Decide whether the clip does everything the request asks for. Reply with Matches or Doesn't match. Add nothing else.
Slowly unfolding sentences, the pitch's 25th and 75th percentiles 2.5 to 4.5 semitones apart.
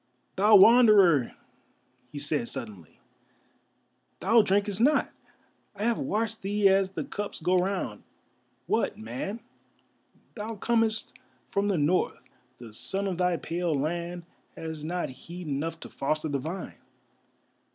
Doesn't match